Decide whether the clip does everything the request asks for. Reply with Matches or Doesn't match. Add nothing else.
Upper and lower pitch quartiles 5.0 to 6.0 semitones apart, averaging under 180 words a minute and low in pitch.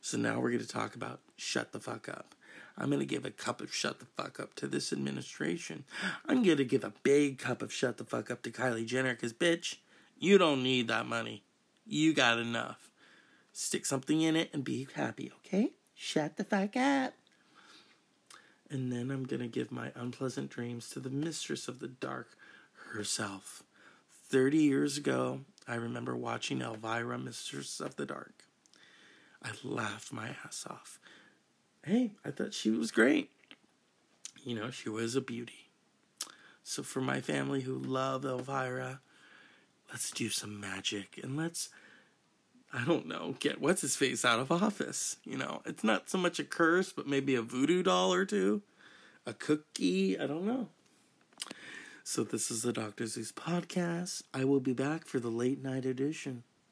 Matches